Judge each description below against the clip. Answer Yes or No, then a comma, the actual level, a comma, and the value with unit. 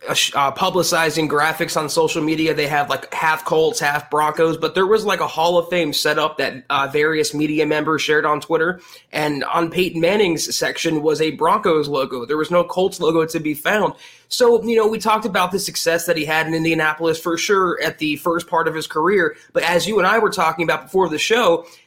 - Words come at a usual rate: No, fast, 220 wpm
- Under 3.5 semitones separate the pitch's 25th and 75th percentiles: Yes, average, 2.9 semitones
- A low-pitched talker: No, medium, 160 Hz